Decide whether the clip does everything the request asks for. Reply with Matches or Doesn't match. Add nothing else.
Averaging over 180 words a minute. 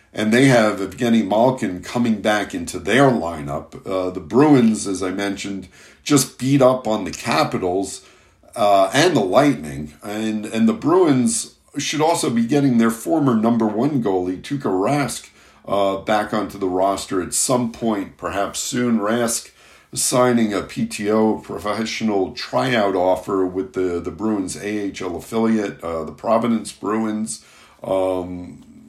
Doesn't match